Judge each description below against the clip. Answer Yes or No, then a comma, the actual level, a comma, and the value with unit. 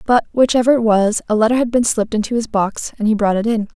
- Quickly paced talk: Yes, fast, 270 wpm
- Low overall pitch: No, high, 225 Hz